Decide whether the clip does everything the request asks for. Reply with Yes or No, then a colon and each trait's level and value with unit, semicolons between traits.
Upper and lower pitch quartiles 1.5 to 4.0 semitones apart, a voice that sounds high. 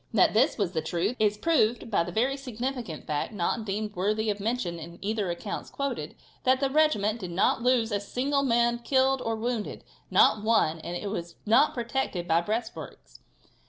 No: average, 4.4 semitones; high, 220 Hz